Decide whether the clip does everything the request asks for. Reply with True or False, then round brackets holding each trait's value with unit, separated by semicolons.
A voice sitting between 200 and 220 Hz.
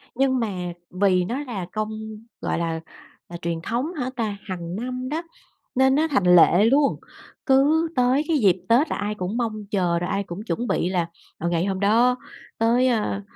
True (215 Hz)